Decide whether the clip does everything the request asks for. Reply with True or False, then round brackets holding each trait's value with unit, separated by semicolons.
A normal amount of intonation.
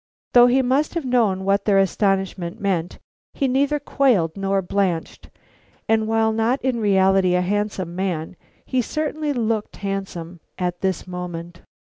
True (4.9 semitones)